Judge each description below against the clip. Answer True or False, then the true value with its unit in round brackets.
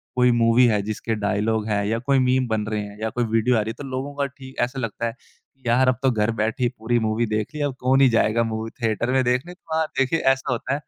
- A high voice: False (120 Hz)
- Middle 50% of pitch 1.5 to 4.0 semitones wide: True (3.0 semitones)